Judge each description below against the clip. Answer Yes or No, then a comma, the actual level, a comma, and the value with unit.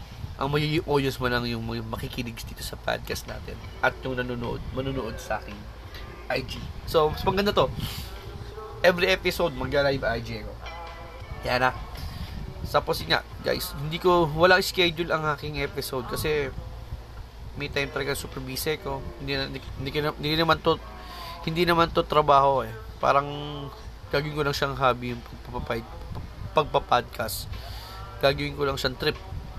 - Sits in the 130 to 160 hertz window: Yes, low, 135 Hz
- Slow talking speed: No, fast, 155 wpm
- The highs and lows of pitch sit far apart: No, average, 4.8 semitones